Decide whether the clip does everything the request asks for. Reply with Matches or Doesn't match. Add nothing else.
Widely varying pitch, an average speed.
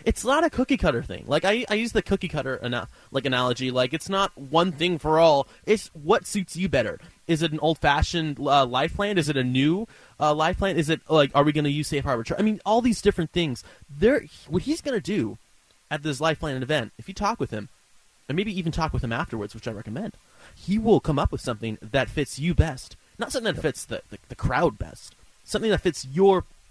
Doesn't match